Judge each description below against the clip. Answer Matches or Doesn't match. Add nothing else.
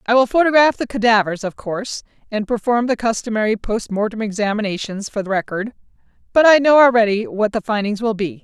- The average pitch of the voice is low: Doesn't match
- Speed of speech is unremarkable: Matches